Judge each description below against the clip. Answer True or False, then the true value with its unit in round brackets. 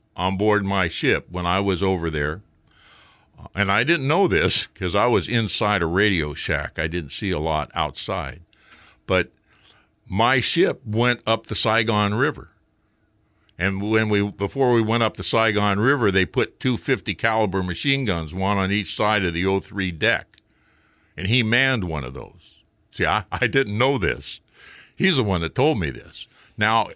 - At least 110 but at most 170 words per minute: False (180 wpm)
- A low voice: True (105 Hz)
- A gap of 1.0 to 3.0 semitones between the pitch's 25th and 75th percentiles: False (3.5 semitones)